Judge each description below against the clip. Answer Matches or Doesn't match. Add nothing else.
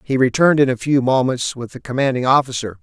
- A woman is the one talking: Doesn't match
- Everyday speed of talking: Doesn't match